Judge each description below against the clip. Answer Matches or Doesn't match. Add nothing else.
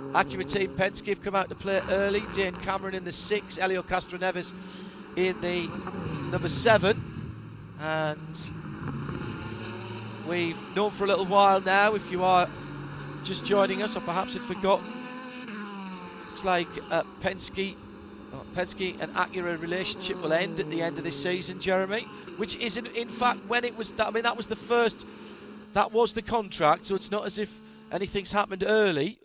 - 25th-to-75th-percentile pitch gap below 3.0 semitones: Matches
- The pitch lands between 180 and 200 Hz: Matches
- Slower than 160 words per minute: Doesn't match